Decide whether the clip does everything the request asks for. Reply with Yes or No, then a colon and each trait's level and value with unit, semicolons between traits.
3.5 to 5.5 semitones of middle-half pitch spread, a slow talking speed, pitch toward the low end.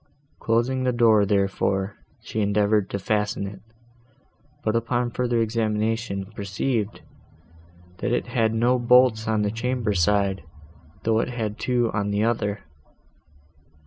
No: narrow, 2.6 semitones; slow, 130 wpm; low, 110 Hz